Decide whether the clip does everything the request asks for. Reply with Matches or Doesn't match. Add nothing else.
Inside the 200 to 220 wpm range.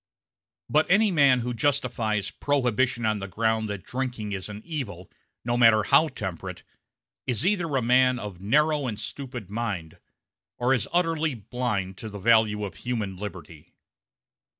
Doesn't match